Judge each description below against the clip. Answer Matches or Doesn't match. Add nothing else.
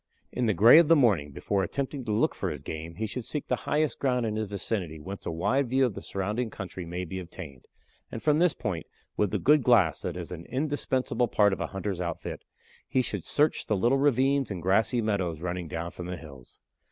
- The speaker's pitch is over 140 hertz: Doesn't match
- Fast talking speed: Matches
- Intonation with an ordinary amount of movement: Doesn't match